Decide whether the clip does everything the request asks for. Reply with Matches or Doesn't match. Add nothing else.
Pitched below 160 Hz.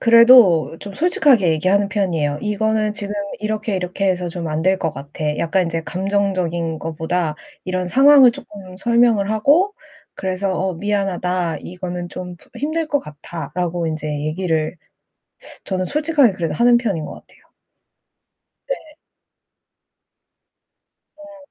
Doesn't match